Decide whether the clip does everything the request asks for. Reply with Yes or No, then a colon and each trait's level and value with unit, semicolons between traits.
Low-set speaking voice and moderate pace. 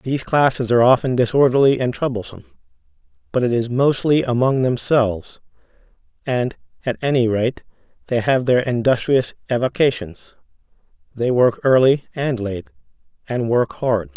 No: low, 125 Hz; slow, 125 wpm